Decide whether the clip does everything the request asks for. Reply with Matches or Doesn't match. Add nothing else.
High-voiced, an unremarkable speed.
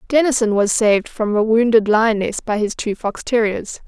Matches